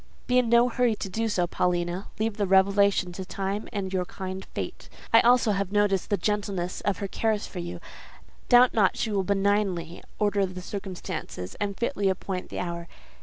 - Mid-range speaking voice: No, high, 195 Hz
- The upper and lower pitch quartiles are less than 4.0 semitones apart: Yes, narrow, 2.4 semitones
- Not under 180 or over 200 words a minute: Yes, average, 185 wpm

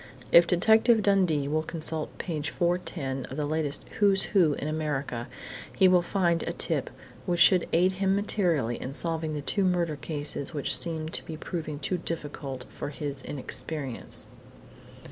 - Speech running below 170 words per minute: Yes, average, 160 wpm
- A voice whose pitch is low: No, medium, 160 Hz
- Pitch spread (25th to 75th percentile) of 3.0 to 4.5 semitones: Yes, average, 3.6 semitones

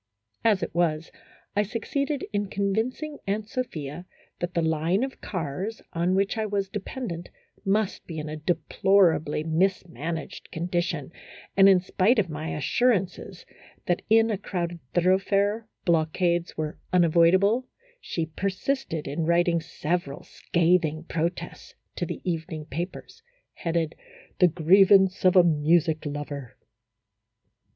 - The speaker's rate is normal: No, slow, 130 wpm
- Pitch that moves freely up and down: No, average, 3.5 semitones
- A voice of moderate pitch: Yes, medium, 175 Hz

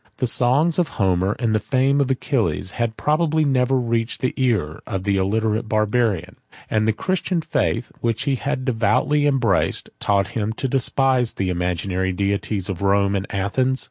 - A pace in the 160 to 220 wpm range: Yes, average, 170 wpm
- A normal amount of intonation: Yes, average, 5.0 semitones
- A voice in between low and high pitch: No, low, 115 Hz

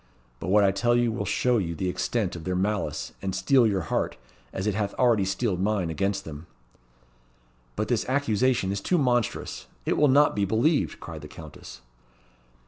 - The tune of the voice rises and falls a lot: No, average, 4.5 semitones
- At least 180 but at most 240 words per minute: Yes, average, 185 wpm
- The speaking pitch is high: No, low, 100 Hz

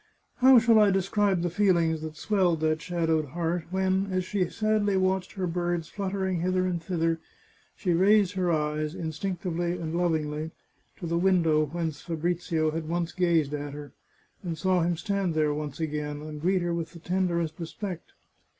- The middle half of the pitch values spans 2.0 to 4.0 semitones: Yes, average, 2.8 semitones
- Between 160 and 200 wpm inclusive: Yes, average, 170 wpm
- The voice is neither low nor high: Yes, medium, 175 Hz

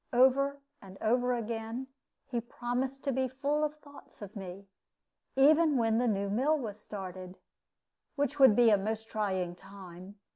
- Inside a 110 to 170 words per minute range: Yes, average, 155 wpm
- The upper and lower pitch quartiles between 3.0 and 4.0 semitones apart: No, average, 5.1 semitones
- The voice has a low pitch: No, high, 235 Hz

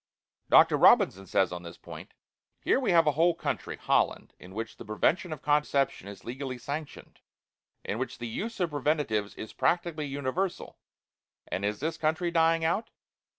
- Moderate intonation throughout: No, wide, 6.6 semitones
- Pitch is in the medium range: Yes, medium, 145 Hz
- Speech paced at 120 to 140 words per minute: No, average, 165 wpm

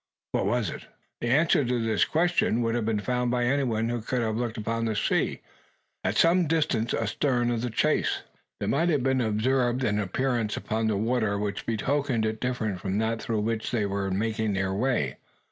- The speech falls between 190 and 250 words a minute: Yes, average, 195 wpm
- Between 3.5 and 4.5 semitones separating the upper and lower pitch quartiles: No, average, 2.8 semitones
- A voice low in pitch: Yes, low, 115 Hz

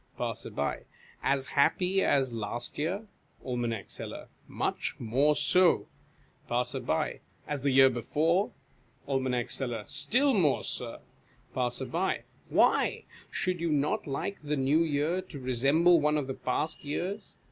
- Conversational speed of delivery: No, slow, 125 wpm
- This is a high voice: No, medium, 145 Hz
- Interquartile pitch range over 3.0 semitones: Yes, average, 4.4 semitones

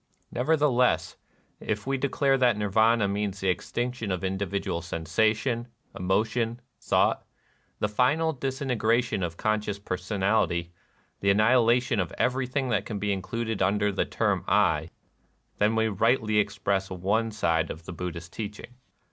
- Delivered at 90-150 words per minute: Yes, average, 140 wpm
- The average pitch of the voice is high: No, low, 105 Hz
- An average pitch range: Yes, average, 3.9 semitones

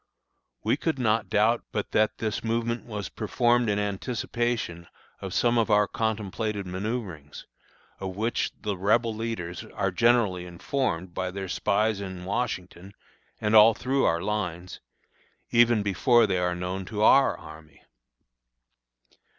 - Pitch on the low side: Yes, low, 105 Hz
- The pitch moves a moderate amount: Yes, average, 3.9 semitones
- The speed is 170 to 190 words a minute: No, slow, 135 wpm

